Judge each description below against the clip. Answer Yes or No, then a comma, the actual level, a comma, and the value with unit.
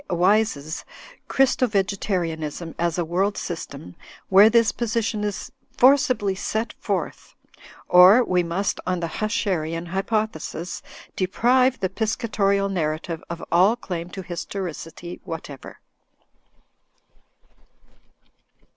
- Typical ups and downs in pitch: Yes, average, 4.1 semitones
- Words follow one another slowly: Yes, slow, 100 wpm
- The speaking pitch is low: No, high, 190 Hz